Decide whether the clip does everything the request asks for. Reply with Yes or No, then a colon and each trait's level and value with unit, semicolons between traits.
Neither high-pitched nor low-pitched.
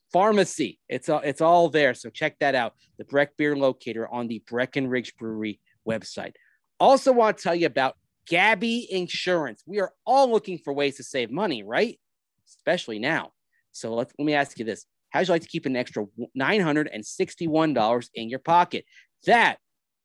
Yes: medium, 145 Hz